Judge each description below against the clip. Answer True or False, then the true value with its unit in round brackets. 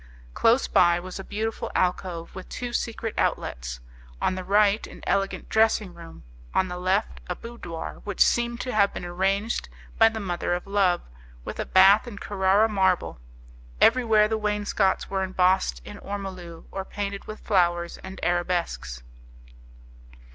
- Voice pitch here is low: False (195 Hz)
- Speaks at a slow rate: False (155 wpm)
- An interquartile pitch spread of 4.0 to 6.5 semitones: False (3.1 semitones)